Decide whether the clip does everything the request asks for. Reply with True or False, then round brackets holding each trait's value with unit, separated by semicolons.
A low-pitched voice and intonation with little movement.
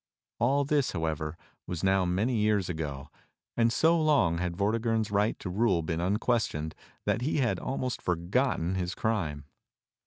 False (100 Hz; 5.6 semitones)